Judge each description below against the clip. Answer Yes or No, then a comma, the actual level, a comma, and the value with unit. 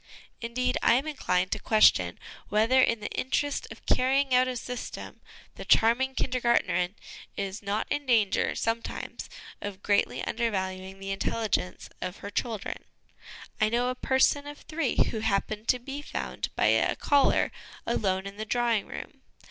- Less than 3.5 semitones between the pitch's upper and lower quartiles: No, average, 4.1 semitones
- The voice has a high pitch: Yes, high, 230 Hz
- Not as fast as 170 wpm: Yes, average, 155 wpm